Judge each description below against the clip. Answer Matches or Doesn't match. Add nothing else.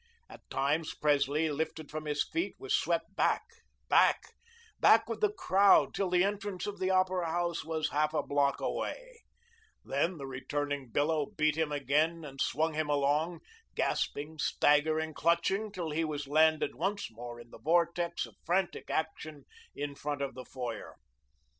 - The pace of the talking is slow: Doesn't match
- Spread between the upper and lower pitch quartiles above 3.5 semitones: Doesn't match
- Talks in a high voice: Doesn't match